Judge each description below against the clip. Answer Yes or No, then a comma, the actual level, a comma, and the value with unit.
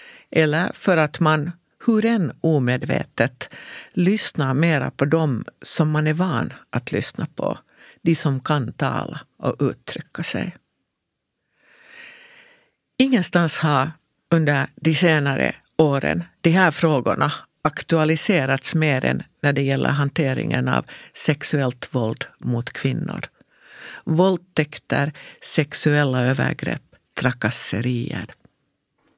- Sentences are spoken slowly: Yes, slow, 105 wpm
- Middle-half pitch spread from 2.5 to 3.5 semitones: No, average, 4.0 semitones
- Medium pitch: Yes, medium, 155 Hz